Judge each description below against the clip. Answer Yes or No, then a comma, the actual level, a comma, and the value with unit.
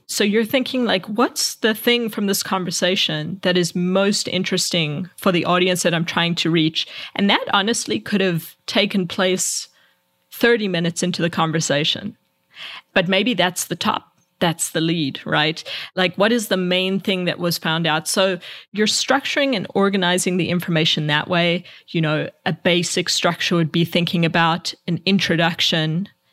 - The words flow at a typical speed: Yes, average, 165 wpm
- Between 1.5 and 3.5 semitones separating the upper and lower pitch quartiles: Yes, average, 2.9 semitones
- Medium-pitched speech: Yes, medium, 180 Hz